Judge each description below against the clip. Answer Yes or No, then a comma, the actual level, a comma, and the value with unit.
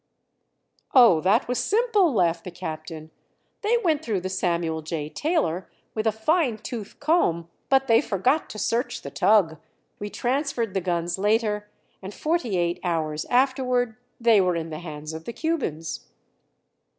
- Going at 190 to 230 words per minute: No, average, 155 wpm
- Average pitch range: No, wide, 7.0 semitones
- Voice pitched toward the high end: Yes, high, 205 Hz